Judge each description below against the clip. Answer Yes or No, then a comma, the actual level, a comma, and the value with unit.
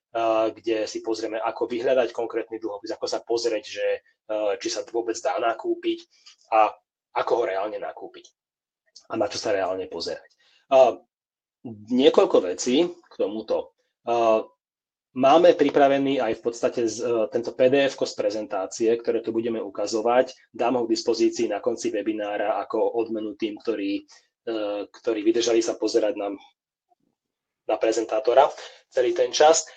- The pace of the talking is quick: No, average, 130 wpm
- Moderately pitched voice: Yes, medium, 145 Hz